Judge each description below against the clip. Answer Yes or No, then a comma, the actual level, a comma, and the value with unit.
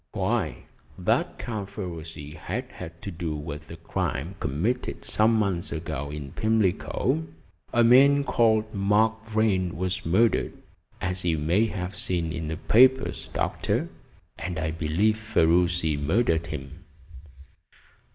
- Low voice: Yes, very low, 90 Hz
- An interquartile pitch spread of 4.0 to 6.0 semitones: Yes, average, 5.2 semitones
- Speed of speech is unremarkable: No, slow, 130 wpm